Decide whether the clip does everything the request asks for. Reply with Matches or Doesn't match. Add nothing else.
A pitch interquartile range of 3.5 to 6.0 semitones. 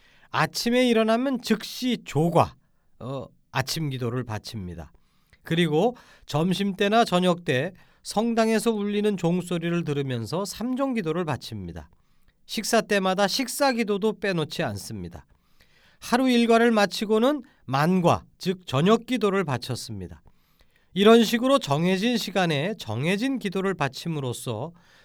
Doesn't match